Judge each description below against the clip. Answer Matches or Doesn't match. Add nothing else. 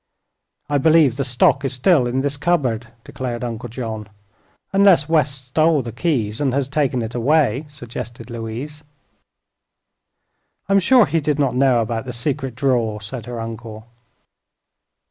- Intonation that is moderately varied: Matches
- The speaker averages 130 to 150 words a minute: Matches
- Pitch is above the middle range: Doesn't match